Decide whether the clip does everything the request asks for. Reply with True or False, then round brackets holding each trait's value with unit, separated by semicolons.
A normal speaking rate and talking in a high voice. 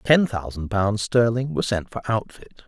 False (180 wpm; 110 Hz)